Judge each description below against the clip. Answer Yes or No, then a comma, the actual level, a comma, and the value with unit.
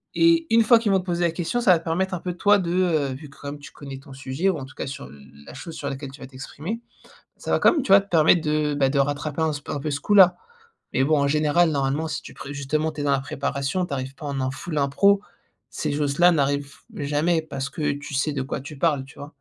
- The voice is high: No, medium, 150 Hz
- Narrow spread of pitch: No, average, 3.8 semitones